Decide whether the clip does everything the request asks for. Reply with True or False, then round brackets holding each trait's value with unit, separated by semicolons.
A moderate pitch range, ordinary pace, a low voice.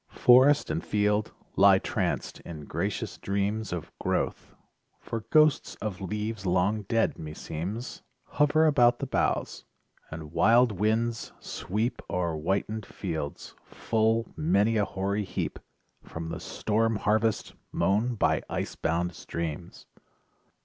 False (4.3 semitones; 125 wpm; 105 Hz)